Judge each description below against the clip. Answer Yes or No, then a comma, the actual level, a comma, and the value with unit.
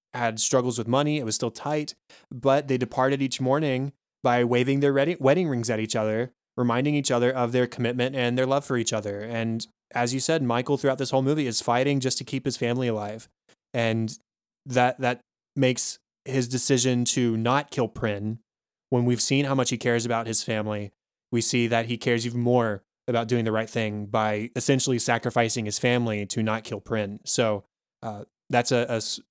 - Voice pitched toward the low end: Yes, low, 120 Hz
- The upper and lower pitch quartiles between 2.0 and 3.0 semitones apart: Yes, narrow, 2.5 semitones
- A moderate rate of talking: Yes, average, 195 wpm